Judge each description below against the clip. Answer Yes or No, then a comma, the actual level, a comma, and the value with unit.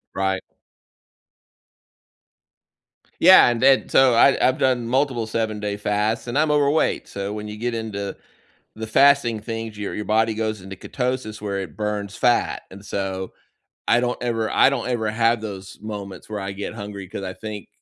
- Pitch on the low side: Yes, low, 110 Hz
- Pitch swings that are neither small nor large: Yes, average, 3.0 semitones